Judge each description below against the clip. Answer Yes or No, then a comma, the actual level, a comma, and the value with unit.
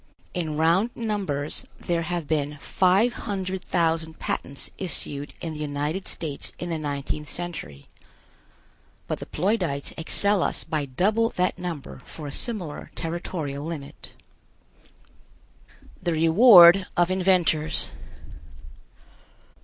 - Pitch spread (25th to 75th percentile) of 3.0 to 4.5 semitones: Yes, average, 3.7 semitones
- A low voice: No, medium, 170 Hz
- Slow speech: Yes, slow, 115 wpm